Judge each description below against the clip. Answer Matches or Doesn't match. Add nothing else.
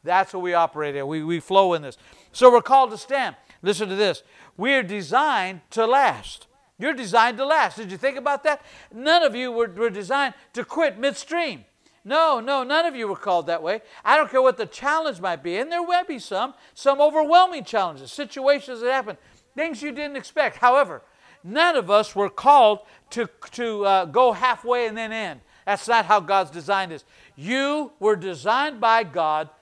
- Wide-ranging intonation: Matches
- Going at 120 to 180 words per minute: Doesn't match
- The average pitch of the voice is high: Matches